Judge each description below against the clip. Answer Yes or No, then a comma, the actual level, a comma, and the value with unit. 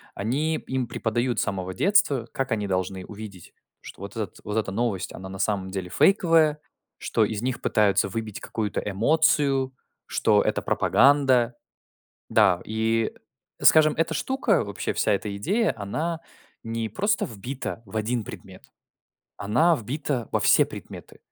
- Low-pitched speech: Yes, low, 115 Hz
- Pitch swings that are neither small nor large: No, wide, 6.0 semitones